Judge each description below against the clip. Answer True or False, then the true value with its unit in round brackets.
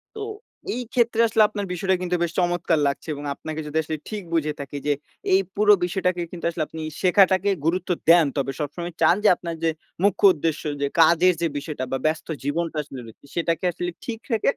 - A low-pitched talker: False (170 Hz)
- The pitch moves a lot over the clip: False (3.3 semitones)